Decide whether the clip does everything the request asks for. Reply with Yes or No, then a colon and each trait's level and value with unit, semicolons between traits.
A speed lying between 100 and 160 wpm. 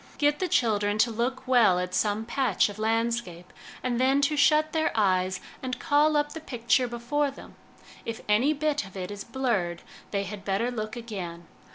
No: average, 185 wpm